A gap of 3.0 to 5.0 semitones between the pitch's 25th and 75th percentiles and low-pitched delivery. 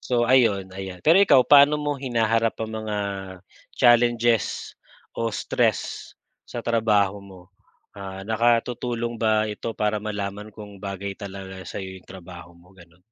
Yes: average, 3.4 semitones; low, 105 Hz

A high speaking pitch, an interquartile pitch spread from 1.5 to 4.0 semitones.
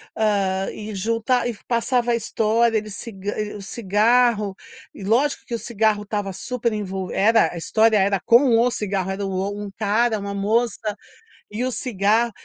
Yes: high, 215 Hz; average, 2.8 semitones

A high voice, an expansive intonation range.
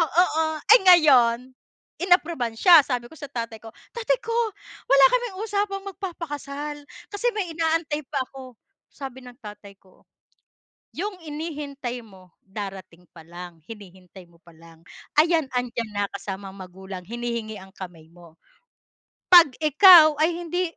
Yes: very high, 260 Hz; wide, 8.9 semitones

